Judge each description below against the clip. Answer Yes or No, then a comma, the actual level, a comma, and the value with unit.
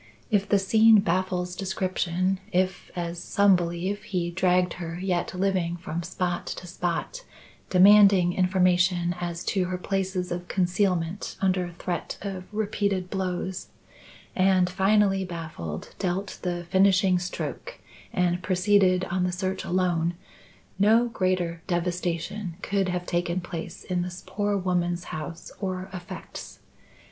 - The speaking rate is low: Yes, slow, 130 wpm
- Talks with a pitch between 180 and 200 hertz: Yes, medium, 185 Hz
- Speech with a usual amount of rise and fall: No, narrow, 1.6 semitones